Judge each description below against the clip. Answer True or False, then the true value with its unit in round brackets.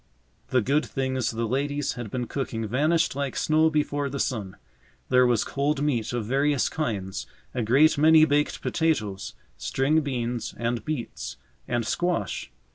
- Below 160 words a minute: True (150 wpm)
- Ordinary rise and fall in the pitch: True (4.0 semitones)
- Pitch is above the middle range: False (135 Hz)